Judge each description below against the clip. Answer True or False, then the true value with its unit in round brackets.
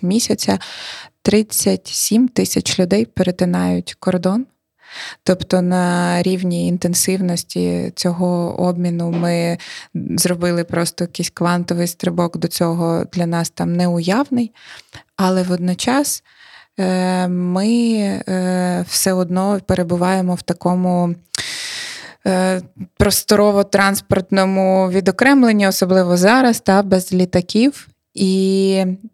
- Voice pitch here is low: False (185 Hz)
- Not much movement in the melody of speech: True (1.9 semitones)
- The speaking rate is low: True (85 wpm)